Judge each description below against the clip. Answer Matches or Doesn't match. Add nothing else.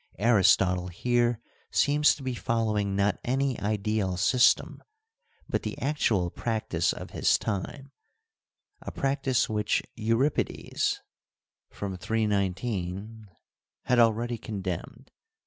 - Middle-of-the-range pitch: Doesn't match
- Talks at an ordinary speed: Doesn't match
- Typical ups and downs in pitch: Matches